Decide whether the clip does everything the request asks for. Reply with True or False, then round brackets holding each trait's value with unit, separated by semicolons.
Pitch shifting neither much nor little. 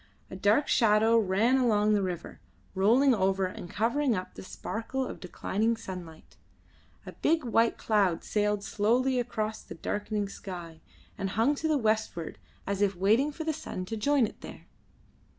True (3.8 semitones)